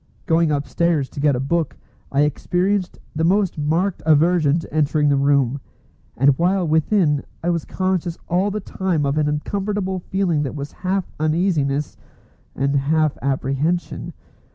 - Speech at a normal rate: Yes, average, 150 wpm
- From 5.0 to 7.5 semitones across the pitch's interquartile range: No, average, 3.9 semitones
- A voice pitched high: No, medium, 160 Hz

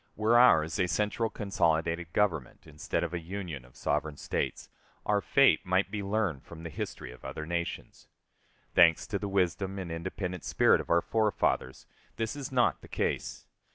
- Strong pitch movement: No, average, 4.2 semitones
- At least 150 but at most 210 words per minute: Yes, average, 170 wpm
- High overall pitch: No, very low, 90 Hz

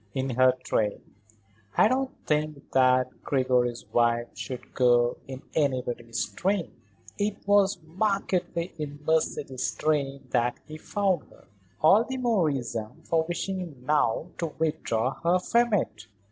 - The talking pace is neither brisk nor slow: No, slow, 130 wpm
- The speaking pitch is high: No, medium, 150 Hz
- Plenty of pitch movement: Yes, wide, 6.3 semitones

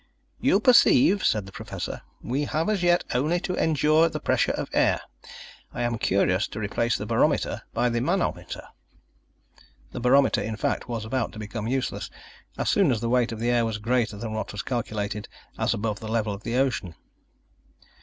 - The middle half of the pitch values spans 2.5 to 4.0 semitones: No, average, 4.6 semitones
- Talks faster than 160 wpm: Yes, average, 185 wpm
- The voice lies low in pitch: Yes, low, 120 Hz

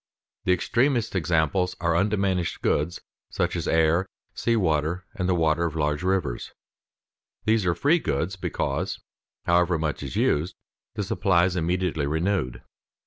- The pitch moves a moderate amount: Yes, average, 3.1 semitones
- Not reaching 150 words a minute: Yes, average, 140 wpm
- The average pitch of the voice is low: Yes, very low, 90 Hz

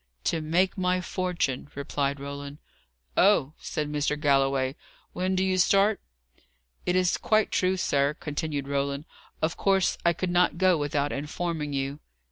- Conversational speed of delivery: Yes, average, 145 wpm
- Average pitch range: Yes, average, 4.4 semitones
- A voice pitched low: No, medium, 155 Hz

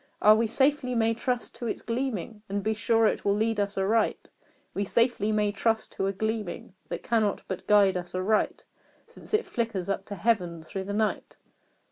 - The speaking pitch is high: Yes, high, 215 Hz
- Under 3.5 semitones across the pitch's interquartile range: Yes, narrow, 2.5 semitones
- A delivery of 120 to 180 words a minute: No, average, 190 wpm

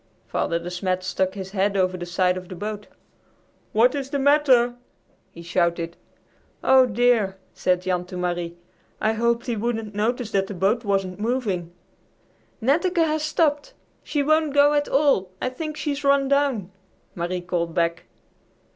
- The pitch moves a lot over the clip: Yes, wide, 7.0 semitones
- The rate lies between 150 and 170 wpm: Yes, average, 160 wpm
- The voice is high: Yes, high, 210 Hz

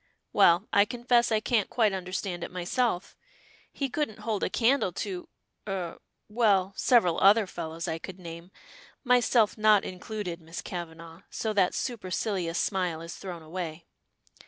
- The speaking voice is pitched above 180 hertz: Yes, high, 190 Hz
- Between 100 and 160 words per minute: Yes, average, 145 wpm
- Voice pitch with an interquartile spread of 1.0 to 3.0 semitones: No, average, 4.1 semitones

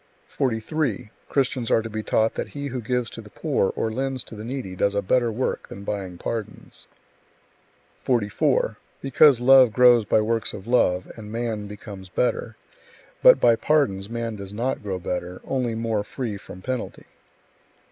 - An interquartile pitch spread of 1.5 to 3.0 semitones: No, average, 3.7 semitones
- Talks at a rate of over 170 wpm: No, average, 165 wpm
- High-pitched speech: No, low, 115 Hz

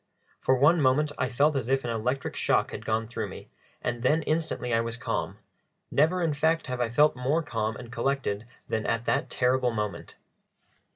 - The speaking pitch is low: Yes, low, 125 Hz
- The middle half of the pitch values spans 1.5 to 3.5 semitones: No, average, 4.2 semitones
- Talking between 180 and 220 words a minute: Yes, average, 190 wpm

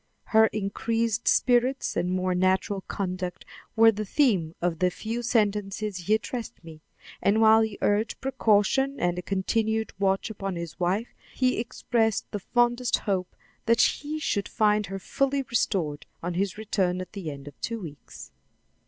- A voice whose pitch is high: Yes, high, 210 Hz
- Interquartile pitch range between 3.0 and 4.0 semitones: Yes, average, 3.7 semitones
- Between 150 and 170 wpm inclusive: Yes, average, 160 wpm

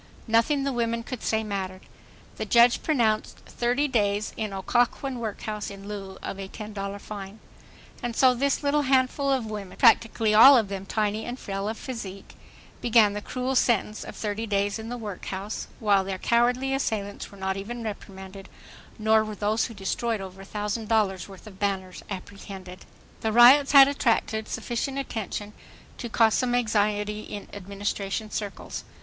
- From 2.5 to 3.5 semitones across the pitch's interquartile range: Yes, average, 3.1 semitones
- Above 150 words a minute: Yes, average, 165 wpm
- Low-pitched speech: No, high, 215 Hz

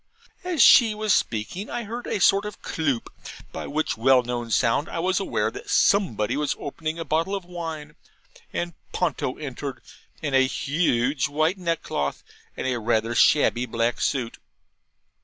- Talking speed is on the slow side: No, average, 160 wpm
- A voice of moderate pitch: Yes, medium, 150 Hz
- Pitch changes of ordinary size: No, wide, 6.5 semitones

